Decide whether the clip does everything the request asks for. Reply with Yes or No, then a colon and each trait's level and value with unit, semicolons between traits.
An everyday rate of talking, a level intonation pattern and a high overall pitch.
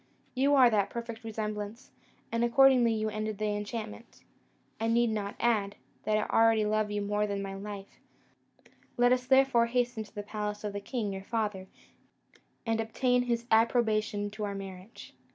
Yes: average, 170 wpm; narrow, 2.3 semitones; high, 215 Hz